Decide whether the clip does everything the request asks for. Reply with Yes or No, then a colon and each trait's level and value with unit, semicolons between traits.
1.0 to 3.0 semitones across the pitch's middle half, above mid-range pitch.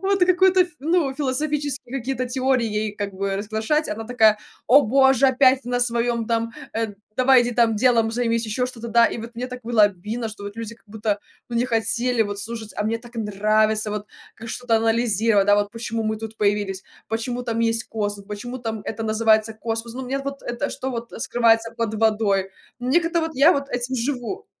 Yes: average, 2.7 semitones; high, 230 Hz